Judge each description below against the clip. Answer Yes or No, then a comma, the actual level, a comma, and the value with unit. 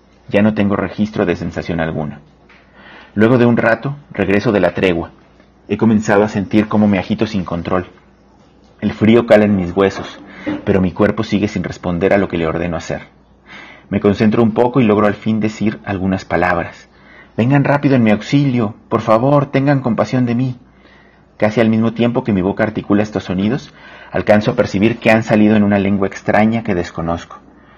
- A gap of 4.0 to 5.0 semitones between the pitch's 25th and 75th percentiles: No, average, 3.0 semitones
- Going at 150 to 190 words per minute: Yes, average, 185 wpm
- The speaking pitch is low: Yes, low, 105 Hz